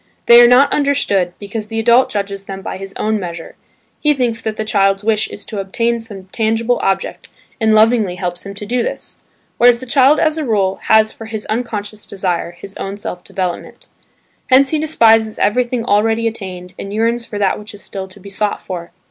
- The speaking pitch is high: Yes, high, 215 Hz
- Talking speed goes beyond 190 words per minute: Yes, average, 200 wpm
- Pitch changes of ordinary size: Yes, average, 3.1 semitones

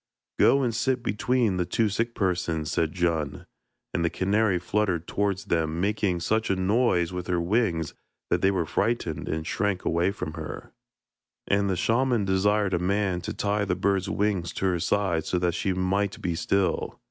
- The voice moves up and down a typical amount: Yes, average, 3.1 semitones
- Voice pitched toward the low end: Yes, very low, 95 Hz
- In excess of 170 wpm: Yes, average, 180 wpm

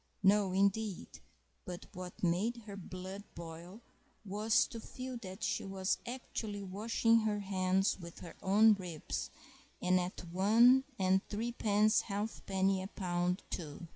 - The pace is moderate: No, slow, 130 wpm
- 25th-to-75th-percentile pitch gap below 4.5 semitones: Yes, average, 2.8 semitones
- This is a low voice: No, high, 195 Hz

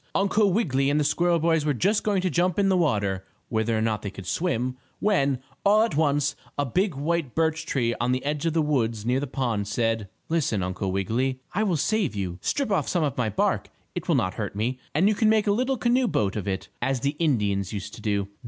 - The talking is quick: Yes, fast, 240 wpm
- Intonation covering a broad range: Yes, wide, 8.0 semitones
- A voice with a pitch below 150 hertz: Yes, medium, 140 Hz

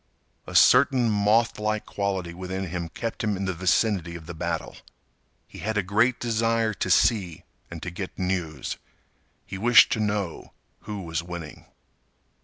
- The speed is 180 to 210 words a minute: No, average, 155 wpm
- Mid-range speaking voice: No, very low, 95 Hz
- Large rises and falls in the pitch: No, average, 3.9 semitones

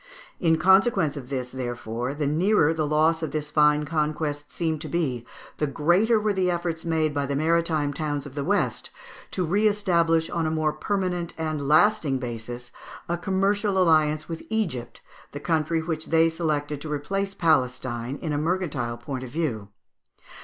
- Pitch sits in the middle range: Yes, medium, 155 Hz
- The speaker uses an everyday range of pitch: Yes, average, 3.1 semitones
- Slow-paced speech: No, average, 170 wpm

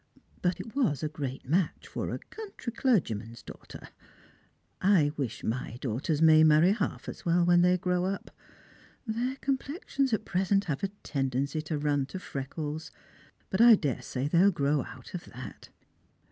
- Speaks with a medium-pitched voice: Yes, medium, 165 Hz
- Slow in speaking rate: No, average, 160 wpm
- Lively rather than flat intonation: Yes, wide, 5.7 semitones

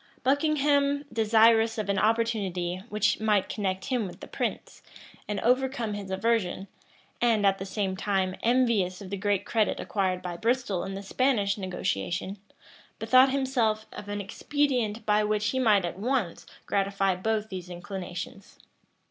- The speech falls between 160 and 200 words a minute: No, average, 150 wpm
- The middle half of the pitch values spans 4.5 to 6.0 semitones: No, average, 3.4 semitones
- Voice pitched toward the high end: Yes, high, 210 Hz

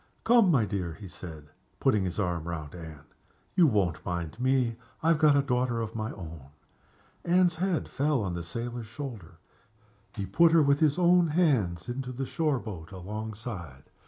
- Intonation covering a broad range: Yes, wide, 8.6 semitones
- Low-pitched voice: Yes, low, 115 Hz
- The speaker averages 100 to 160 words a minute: No, average, 175 wpm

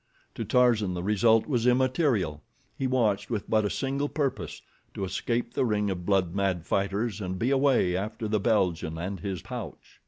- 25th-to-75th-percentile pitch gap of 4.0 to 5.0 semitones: Yes, average, 4.6 semitones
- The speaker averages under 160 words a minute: No, average, 175 wpm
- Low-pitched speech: Yes, low, 105 Hz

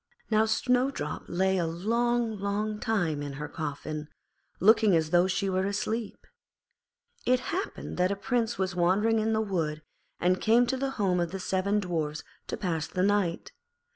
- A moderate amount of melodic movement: Yes, average, 4.3 semitones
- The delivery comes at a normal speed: Yes, average, 170 wpm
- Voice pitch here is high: Yes, high, 195 Hz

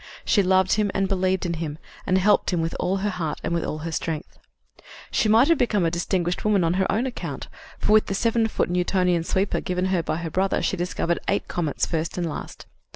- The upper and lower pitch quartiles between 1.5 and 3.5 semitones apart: Yes, average, 2.8 semitones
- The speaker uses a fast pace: Yes, fast, 225 wpm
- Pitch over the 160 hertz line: Yes, medium, 185 Hz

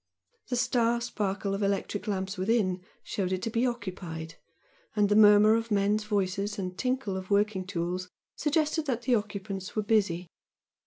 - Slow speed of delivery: No, average, 160 wpm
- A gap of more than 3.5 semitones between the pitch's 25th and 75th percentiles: No, average, 3.2 semitones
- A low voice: No, high, 205 Hz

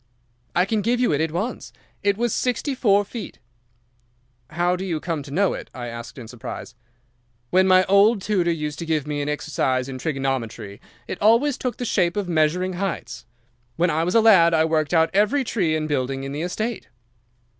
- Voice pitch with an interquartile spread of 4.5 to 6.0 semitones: Yes, wide, 5.4 semitones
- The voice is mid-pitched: Yes, medium, 170 Hz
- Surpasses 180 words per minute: Yes, average, 200 wpm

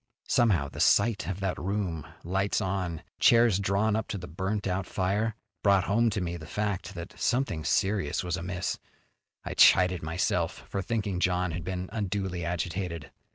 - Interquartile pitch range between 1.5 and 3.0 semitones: Yes, narrow, 2.5 semitones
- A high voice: No, very low, 95 Hz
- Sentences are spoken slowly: No, average, 165 wpm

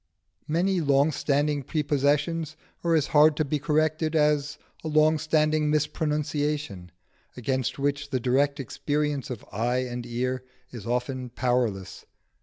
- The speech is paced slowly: Yes, slow, 130 wpm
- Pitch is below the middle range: No, medium, 145 Hz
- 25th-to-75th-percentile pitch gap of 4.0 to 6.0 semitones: No, average, 3.1 semitones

